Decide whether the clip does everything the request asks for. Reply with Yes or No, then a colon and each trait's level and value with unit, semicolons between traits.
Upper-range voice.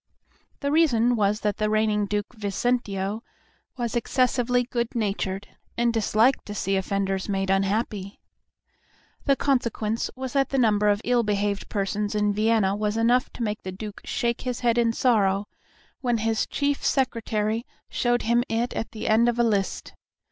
Yes: high, 220 Hz